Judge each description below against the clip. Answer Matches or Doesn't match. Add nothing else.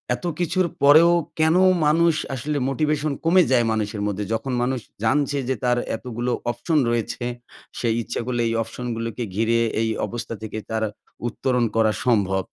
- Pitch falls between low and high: Doesn't match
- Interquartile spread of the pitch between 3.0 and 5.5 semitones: Matches